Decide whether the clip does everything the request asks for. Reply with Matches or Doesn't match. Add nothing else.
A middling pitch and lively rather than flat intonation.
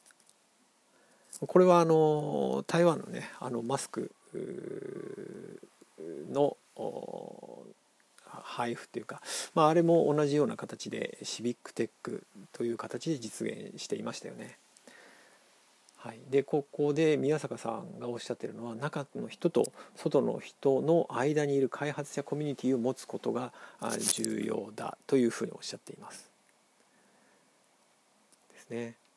Doesn't match